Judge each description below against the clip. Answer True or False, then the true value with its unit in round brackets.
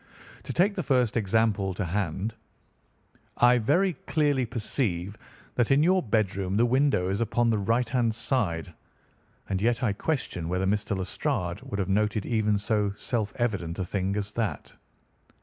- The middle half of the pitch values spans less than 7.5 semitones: True (3.9 semitones)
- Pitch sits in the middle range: False (110 Hz)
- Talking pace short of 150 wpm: False (160 wpm)